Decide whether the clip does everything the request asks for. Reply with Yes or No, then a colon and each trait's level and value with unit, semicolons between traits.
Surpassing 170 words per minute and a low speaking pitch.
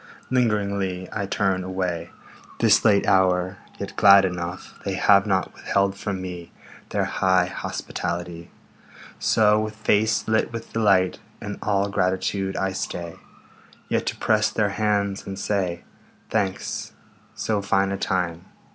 No: slow, 135 wpm; very low, 95 Hz